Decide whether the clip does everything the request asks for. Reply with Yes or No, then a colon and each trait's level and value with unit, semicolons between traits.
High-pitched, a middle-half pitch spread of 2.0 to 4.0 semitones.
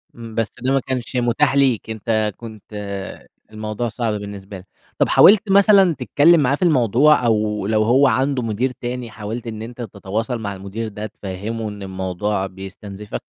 No: low, 115 Hz; average, 3.6 semitones